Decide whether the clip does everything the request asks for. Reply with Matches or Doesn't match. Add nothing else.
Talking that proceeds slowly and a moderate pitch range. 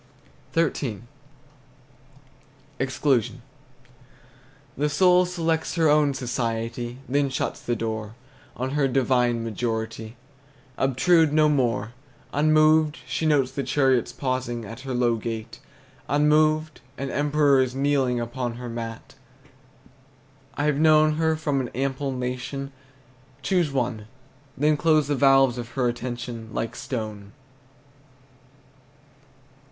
Matches